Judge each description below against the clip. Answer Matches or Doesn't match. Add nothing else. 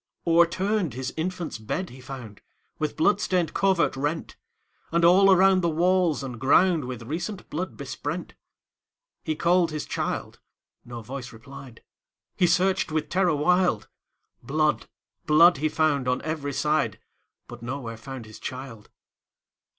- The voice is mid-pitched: Matches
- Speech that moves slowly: Matches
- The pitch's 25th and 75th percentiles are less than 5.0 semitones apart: Doesn't match